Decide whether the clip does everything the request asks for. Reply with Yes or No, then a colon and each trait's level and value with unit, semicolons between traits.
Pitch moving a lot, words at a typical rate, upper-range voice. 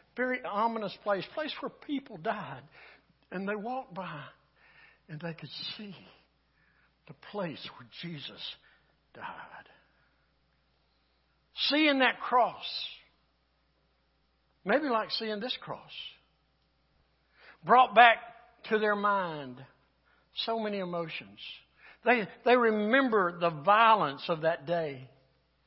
No: wide, 7.8 semitones; slow, 105 wpm; high, 200 Hz